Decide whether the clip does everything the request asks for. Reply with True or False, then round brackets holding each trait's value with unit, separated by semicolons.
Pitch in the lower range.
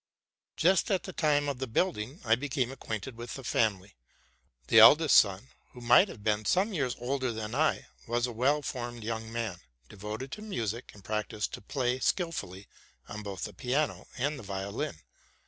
True (120 Hz)